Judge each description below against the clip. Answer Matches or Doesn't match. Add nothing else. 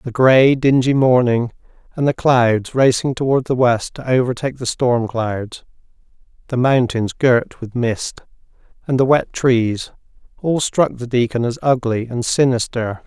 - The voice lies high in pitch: Doesn't match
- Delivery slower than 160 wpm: Matches